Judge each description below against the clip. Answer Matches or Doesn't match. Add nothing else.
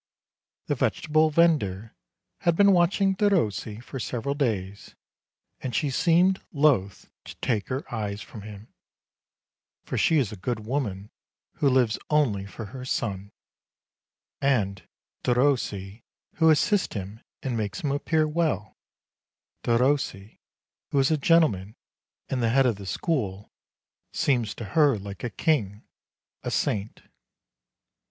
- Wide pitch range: Matches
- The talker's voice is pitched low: Matches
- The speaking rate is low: Matches